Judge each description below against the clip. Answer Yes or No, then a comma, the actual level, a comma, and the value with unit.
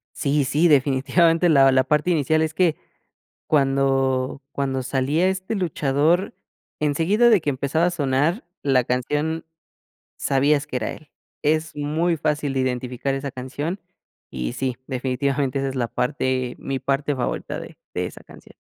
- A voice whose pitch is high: No, medium, 140 Hz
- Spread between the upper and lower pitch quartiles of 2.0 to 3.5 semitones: Yes, average, 3.2 semitones